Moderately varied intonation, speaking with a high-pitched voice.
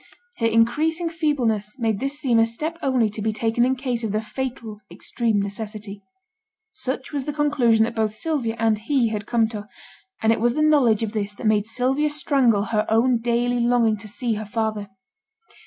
Yes: average, 3.3 semitones; high, 230 Hz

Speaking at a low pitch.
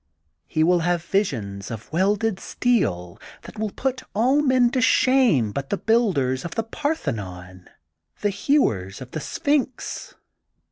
No: high, 190 Hz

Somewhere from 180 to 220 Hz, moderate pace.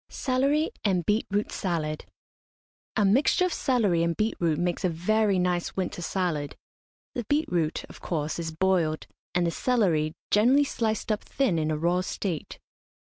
Yes: medium, 185 Hz; average, 165 wpm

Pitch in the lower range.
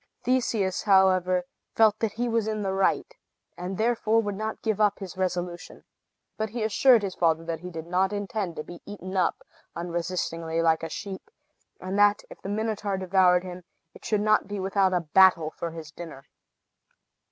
No: high, 190 Hz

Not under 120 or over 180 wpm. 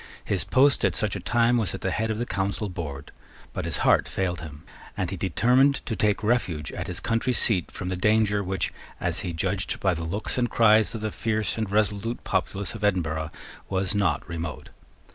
No: fast, 205 wpm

